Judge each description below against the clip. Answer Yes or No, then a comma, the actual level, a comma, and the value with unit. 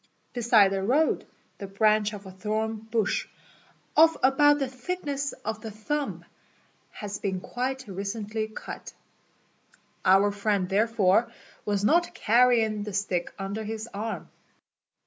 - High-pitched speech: Yes, high, 215 Hz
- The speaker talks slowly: Yes, slow, 130 wpm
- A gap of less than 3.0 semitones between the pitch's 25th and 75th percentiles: No, average, 3.4 semitones